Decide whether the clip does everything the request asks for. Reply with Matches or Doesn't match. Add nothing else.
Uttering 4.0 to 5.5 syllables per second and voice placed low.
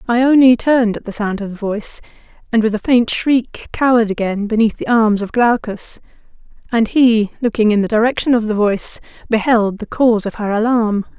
Doesn't match